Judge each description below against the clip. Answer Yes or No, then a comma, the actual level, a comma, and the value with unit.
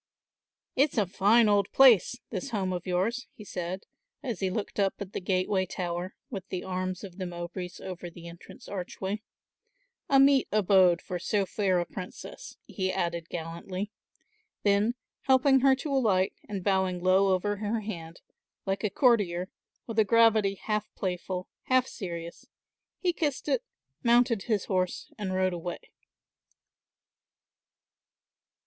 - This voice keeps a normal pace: Yes, average, 145 wpm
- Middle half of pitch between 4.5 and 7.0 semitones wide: No, average, 3.3 semitones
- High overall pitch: Yes, high, 195 Hz